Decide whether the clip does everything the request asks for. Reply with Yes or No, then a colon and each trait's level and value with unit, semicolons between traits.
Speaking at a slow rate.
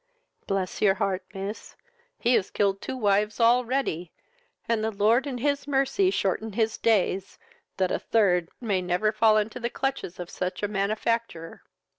No: average, 160 wpm